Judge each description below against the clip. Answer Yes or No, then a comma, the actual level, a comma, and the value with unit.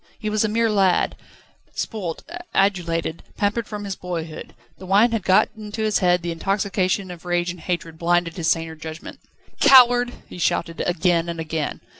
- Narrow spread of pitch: No, average, 3.7 semitones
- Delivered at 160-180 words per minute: Yes, average, 170 wpm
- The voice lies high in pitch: No, medium, 180 Hz